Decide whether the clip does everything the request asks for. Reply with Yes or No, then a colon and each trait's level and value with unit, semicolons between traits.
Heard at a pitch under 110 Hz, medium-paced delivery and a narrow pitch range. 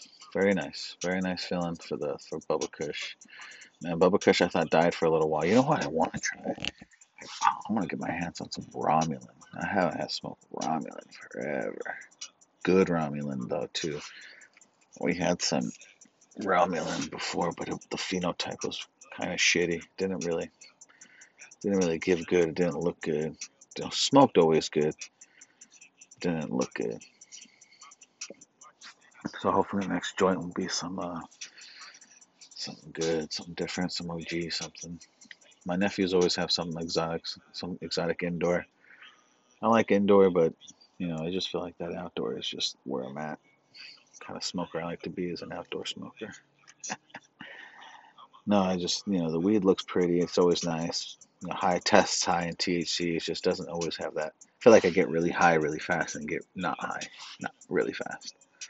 Yes: very low, 85 Hz; average, 170 wpm; narrow, 1.8 semitones